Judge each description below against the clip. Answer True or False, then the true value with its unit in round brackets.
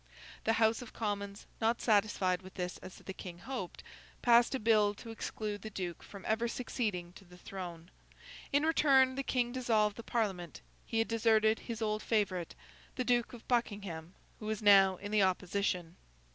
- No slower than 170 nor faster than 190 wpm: True (175 wpm)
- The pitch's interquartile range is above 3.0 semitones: True (3.5 semitones)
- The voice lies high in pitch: True (215 Hz)